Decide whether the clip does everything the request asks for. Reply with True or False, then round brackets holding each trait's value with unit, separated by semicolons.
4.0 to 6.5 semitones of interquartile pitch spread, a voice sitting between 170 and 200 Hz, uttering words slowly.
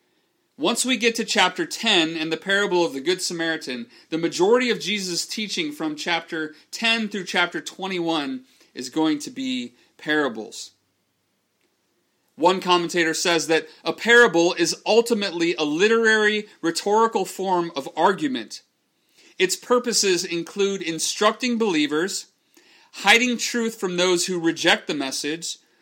True (5.6 semitones; 185 Hz; 130 wpm)